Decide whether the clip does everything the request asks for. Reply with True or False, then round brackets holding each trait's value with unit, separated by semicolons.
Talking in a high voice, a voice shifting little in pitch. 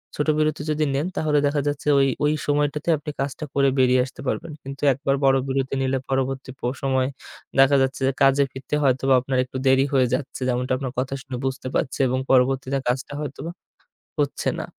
False (135 Hz; 1.5 semitones)